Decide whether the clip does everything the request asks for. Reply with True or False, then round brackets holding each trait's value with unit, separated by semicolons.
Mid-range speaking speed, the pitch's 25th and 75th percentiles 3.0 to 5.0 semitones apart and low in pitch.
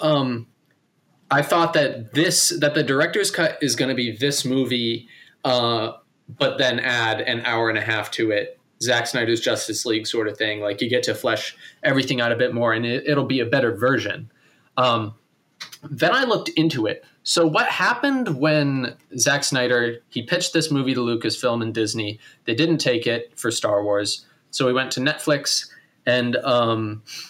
True (185 wpm; 3.8 semitones; 125 Hz)